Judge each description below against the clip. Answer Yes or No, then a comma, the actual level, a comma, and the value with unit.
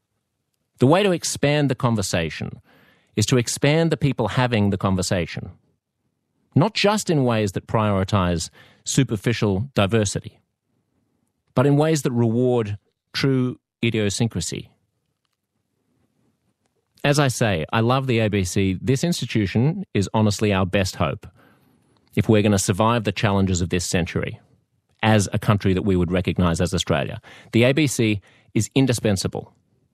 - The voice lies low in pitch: Yes, low, 110 Hz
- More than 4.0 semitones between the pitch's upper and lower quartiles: Yes, average, 4.5 semitones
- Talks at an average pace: No, slow, 130 wpm